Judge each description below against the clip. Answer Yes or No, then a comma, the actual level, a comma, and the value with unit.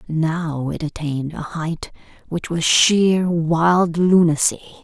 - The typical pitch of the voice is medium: Yes, medium, 165 Hz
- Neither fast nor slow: No, slow, 125 wpm